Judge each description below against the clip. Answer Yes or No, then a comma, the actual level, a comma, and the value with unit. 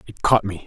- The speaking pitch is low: Yes, low, 100 Hz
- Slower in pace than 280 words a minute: Yes, fast, 270 wpm